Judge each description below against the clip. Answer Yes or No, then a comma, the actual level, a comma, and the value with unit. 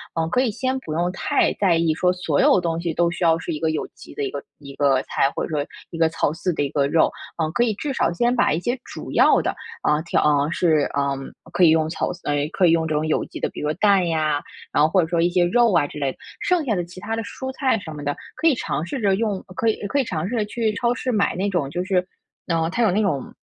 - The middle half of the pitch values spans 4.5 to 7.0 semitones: Yes, average, 5.2 semitones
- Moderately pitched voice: Yes, medium, 175 Hz